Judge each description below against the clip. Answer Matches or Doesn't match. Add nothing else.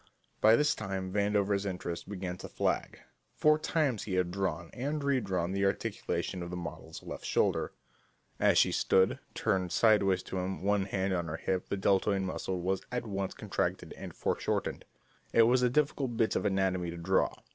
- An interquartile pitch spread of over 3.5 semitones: Doesn't match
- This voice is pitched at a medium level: Doesn't match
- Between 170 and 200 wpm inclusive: Matches